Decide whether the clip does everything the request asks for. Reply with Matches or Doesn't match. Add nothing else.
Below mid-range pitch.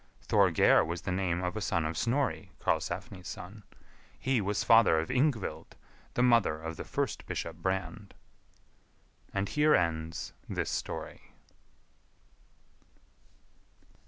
Matches